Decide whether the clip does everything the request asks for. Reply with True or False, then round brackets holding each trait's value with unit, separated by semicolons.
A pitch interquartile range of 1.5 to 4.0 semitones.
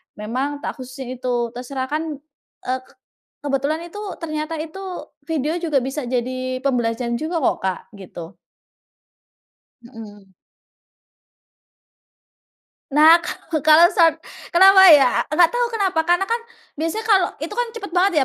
False (5.0 semitones)